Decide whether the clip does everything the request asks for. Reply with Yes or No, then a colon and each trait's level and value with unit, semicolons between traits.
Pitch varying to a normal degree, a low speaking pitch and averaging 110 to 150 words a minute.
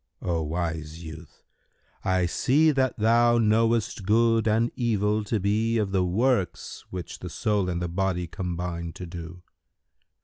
Yes: average, 4.6 semitones; very low, 95 Hz; average, 145 wpm